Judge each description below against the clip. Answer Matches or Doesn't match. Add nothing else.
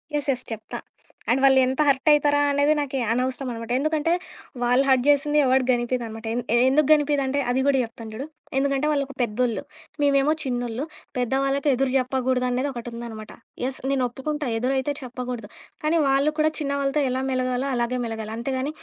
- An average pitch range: Doesn't match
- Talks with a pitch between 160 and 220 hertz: Doesn't match